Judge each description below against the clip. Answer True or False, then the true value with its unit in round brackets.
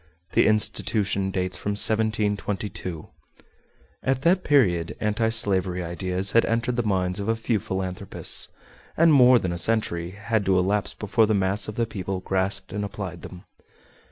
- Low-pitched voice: True (100 Hz)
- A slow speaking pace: False (155 wpm)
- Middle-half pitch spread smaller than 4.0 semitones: True (3.2 semitones)